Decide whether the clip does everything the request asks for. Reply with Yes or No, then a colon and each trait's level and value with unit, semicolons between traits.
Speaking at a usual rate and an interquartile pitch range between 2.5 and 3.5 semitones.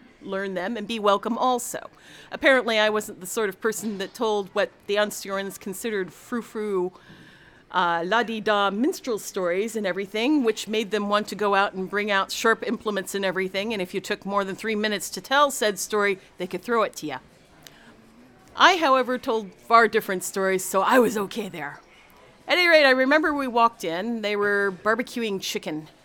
Yes: average, 195 wpm; average, 2.9 semitones